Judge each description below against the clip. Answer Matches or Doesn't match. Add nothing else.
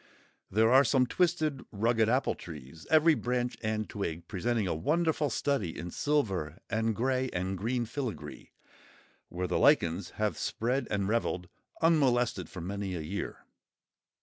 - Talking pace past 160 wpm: Doesn't match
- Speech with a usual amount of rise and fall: Doesn't match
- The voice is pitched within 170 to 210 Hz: Doesn't match